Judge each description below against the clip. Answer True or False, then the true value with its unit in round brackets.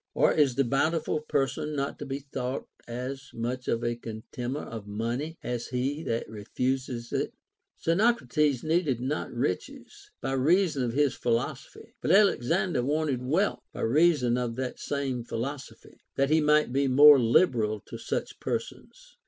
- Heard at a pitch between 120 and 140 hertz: True (135 Hz)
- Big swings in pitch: False (3.8 semitones)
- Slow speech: False (160 wpm)